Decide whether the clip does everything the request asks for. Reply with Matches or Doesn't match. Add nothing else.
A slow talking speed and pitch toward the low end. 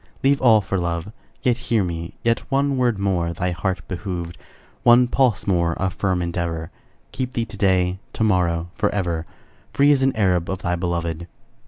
Doesn't match